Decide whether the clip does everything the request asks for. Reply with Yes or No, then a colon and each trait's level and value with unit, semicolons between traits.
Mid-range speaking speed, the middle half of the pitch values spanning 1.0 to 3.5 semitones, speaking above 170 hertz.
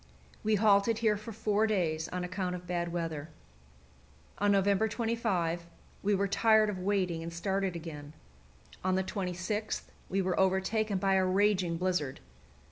Yes: average, 150 wpm; average, 2.8 semitones; high, 190 Hz